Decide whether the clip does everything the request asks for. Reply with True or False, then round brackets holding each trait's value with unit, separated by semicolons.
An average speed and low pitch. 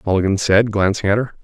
False (210 wpm; 105 Hz)